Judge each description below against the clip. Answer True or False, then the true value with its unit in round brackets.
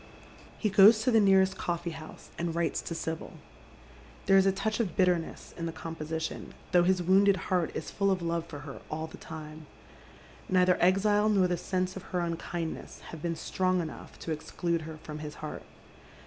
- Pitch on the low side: False (175 Hz)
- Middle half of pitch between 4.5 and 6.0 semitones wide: False (2.9 semitones)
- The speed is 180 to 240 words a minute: True (190 wpm)